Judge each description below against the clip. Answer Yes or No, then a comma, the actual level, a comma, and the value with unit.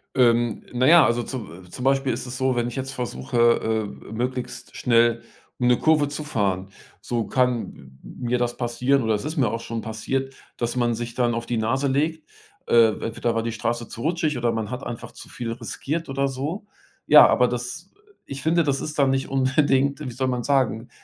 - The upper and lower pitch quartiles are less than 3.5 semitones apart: Yes, average, 2.7 semitones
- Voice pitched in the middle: No, low, 125 Hz